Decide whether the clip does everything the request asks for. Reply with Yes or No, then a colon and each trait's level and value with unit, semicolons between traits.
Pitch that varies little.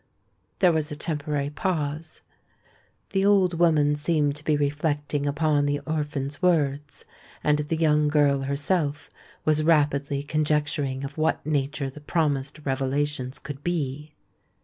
Yes: narrow, 1.5 semitones